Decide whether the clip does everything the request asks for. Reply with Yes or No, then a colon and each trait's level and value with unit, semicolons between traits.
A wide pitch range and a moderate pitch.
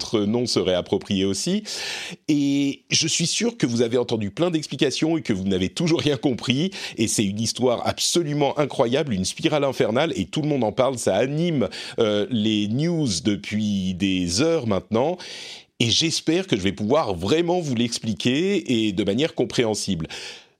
No: wide, 7.3 semitones; low, 125 Hz